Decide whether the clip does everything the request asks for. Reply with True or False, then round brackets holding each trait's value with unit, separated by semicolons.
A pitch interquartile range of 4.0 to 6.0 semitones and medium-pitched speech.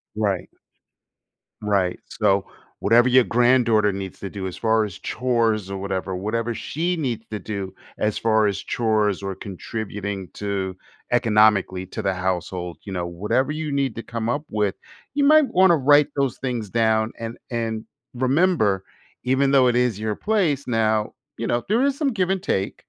False (4.6 semitones; 110 Hz)